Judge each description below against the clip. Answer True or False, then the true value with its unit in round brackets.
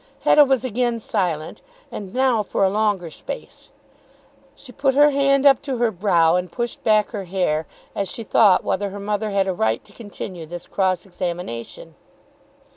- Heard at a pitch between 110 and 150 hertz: False (205 Hz)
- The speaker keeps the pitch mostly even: False (5.0 semitones)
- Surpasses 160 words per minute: True (175 wpm)